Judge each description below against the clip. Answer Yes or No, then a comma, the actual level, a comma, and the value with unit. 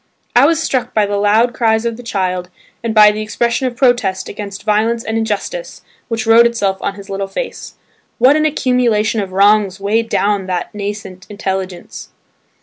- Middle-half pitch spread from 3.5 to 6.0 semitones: No, average, 2.9 semitones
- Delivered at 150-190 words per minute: Yes, average, 175 wpm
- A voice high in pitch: Yes, high, 215 Hz